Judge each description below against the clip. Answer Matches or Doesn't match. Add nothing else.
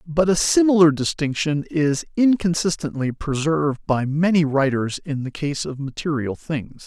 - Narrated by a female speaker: Doesn't match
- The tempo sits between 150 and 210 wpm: Doesn't match